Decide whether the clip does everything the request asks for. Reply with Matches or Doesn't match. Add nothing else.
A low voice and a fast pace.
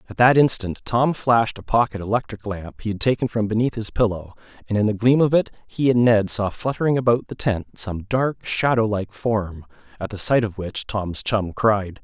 Matches